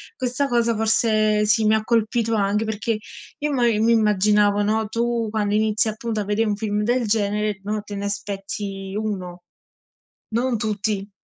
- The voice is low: No, high, 215 Hz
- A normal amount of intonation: No, narrow, 1.7 semitones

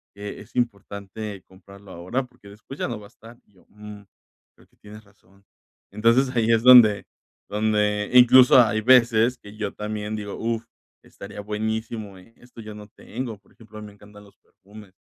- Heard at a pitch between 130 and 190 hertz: No, low, 105 Hz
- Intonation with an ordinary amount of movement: No, narrow, 2.2 semitones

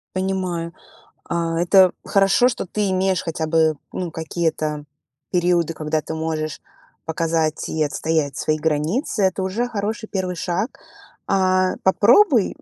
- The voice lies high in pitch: No, medium, 175 Hz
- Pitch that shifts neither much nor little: Yes, average, 3.1 semitones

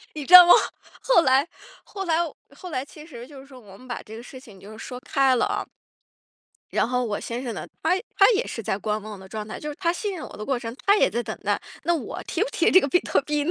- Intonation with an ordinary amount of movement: No, wide, 6.6 semitones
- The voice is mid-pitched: No, very high, 265 Hz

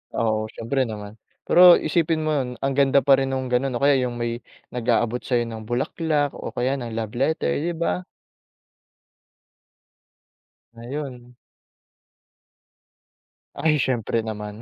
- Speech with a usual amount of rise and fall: Yes, average, 3.5 semitones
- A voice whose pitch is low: Yes, low, 125 Hz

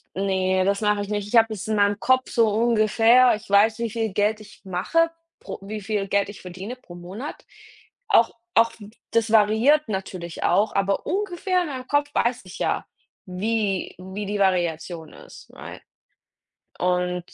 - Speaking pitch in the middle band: No, high, 210 Hz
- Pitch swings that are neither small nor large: Yes, average, 3.2 semitones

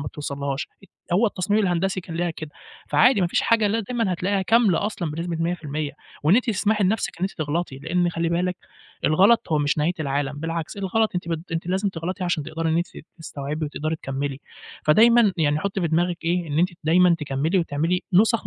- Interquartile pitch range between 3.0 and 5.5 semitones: Yes, average, 3.7 semitones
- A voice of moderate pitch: Yes, medium, 170 Hz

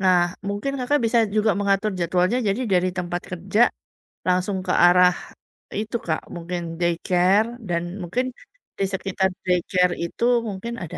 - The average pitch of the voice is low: No, medium, 185 Hz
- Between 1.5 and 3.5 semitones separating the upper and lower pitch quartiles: Yes, narrow, 2.6 semitones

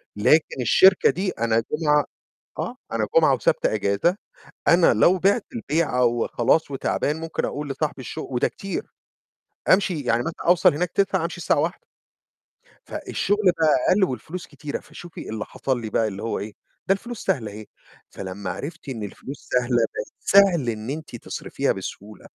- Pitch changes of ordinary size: No, wide, 7.2 semitones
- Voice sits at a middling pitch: Yes, medium, 150 Hz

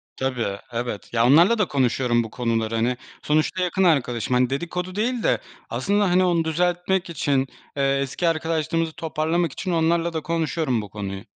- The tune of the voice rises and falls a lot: Yes, wide, 5.7 semitones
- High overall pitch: No, medium, 155 Hz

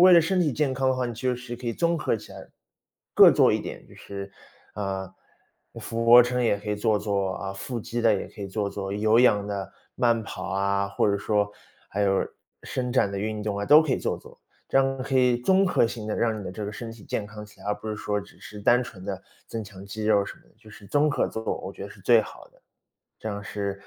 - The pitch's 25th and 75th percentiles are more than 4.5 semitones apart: No, average, 3.3 semitones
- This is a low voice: Yes, low, 105 Hz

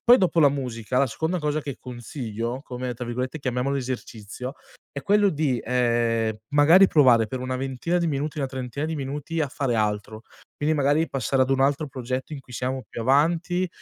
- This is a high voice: No, low, 135 Hz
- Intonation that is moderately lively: Yes, average, 3.2 semitones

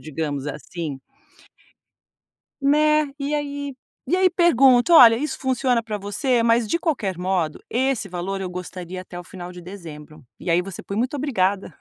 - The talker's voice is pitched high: Yes, high, 205 Hz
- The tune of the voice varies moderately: No, wide, 7.4 semitones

